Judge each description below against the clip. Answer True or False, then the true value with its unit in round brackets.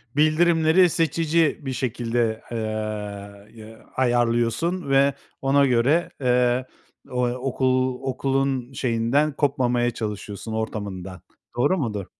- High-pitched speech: False (130 Hz)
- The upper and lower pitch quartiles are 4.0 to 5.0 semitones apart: False (3.3 semitones)